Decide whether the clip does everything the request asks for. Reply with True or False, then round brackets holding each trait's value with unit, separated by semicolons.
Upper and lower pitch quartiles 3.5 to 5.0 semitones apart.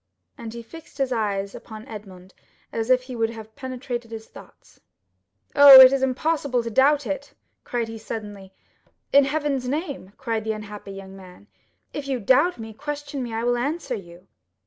True (4.2 semitones)